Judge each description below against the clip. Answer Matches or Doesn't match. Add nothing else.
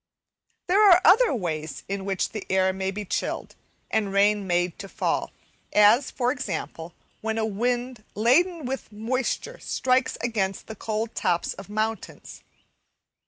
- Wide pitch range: Doesn't match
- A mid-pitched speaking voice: Doesn't match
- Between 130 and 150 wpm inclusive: Matches